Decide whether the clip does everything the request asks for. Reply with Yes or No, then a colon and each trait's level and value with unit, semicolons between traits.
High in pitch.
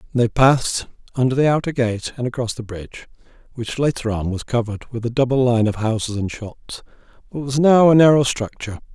No: low, 125 Hz